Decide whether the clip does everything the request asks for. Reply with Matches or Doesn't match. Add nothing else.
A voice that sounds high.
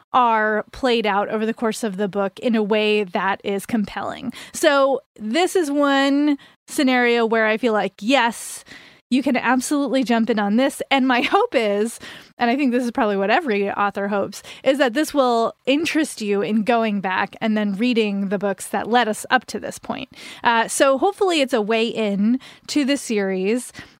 Matches